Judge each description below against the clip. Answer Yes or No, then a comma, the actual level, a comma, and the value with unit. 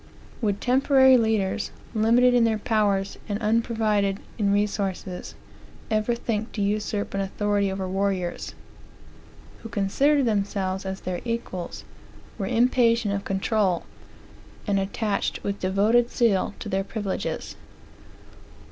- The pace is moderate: No, slow, 120 wpm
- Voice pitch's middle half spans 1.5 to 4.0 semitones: Yes, average, 2.8 semitones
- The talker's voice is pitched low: No, high, 205 Hz